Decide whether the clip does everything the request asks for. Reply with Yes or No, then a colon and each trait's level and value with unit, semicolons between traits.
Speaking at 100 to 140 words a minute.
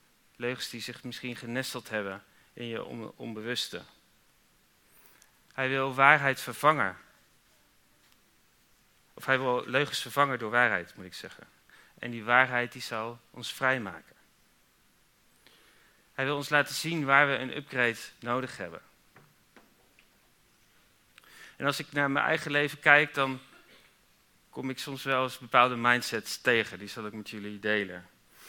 Yes: slow, 135 wpm